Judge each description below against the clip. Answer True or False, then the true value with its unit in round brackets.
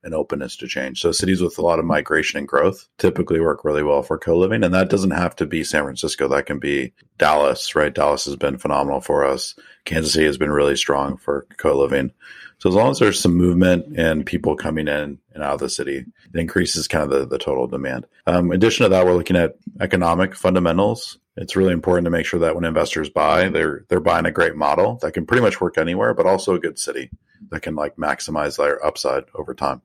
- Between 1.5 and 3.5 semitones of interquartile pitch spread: False (3.9 semitones)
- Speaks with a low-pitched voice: True (90 Hz)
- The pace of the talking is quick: True (230 wpm)